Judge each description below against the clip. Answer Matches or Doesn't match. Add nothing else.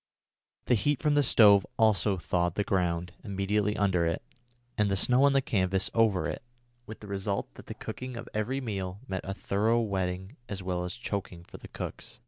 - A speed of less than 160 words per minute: Doesn't match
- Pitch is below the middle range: Matches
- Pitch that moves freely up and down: Doesn't match